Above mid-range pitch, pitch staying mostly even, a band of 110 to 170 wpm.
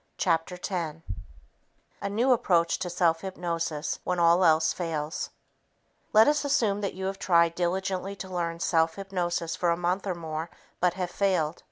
No: medium, 175 Hz; narrow, 2.3 semitones; average, 165 wpm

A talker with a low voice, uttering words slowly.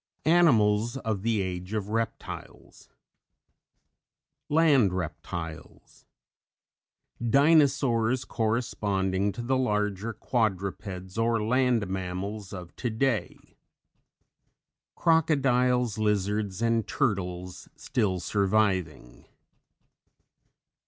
Yes: low, 110 Hz; slow, 70 wpm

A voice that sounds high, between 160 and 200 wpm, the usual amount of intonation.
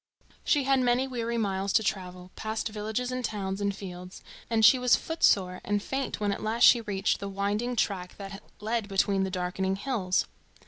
Yes: high, 205 Hz; average, 185 wpm; average, 3.4 semitones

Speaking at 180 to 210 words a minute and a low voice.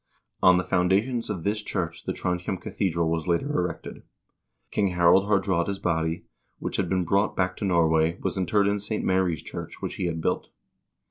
Yes: average, 185 wpm; very low, 90 Hz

